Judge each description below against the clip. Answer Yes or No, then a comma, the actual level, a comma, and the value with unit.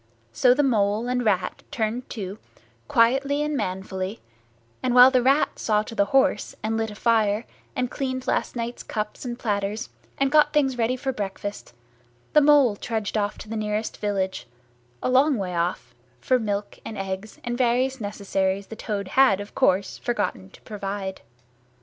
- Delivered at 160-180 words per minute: Yes, average, 170 wpm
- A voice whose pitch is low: No, high, 220 Hz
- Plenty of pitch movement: No, average, 4.0 semitones